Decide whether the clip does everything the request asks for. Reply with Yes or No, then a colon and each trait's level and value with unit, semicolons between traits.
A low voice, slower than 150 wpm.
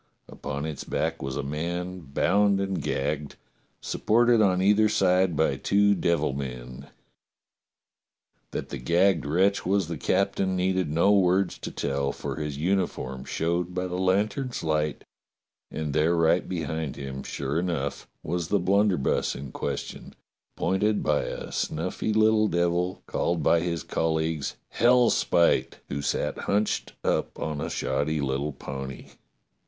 Yes: very low, 85 Hz; average, 140 wpm